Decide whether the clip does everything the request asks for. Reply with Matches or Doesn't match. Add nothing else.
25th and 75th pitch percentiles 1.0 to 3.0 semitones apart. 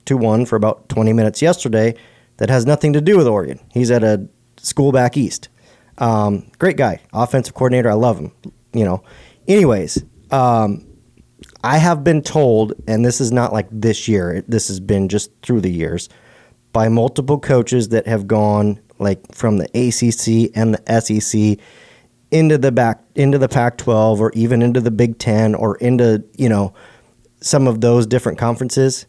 Matches